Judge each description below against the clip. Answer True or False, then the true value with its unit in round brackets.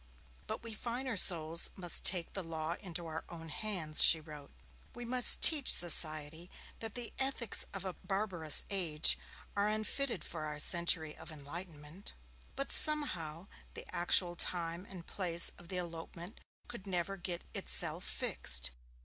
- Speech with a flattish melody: False (3.9 semitones)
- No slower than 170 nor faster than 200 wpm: False (150 wpm)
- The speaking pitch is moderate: True (175 Hz)